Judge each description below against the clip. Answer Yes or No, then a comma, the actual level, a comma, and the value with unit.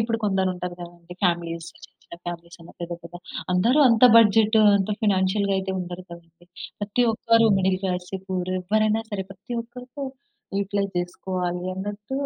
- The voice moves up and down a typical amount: Yes, average, 3.4 semitones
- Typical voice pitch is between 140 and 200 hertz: Yes, high, 190 Hz